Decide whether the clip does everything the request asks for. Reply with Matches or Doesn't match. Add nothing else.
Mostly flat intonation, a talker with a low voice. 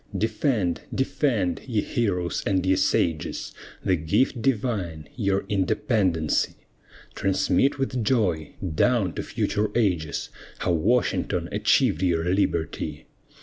Doesn't match